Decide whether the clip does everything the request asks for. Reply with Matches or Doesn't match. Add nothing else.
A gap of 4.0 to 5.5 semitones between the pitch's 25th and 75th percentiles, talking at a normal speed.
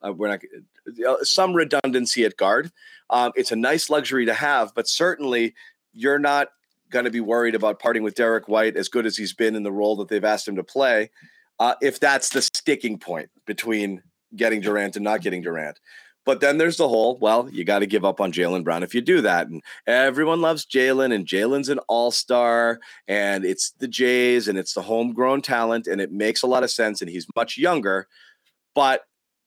Doesn't match